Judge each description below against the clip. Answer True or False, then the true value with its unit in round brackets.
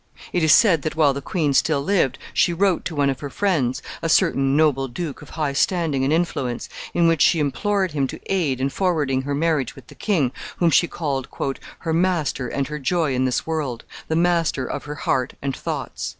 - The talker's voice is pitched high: False (150 Hz)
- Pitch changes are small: False (3.8 semitones)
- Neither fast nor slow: False (210 wpm)